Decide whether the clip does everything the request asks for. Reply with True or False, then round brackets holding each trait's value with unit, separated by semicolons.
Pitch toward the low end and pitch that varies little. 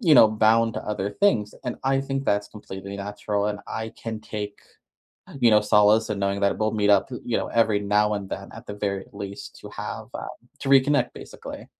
True (105 Hz; 2.0 semitones)